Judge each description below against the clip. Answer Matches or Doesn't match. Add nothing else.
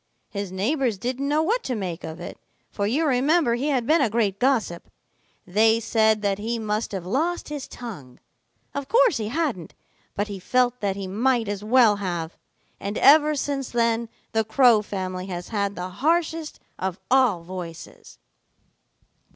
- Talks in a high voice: Matches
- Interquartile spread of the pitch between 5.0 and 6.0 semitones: Matches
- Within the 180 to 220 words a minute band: Doesn't match